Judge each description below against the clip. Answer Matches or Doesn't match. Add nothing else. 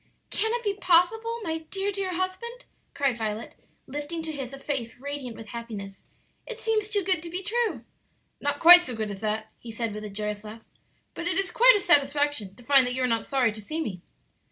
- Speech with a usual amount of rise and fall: Doesn't match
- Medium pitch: Doesn't match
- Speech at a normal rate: Doesn't match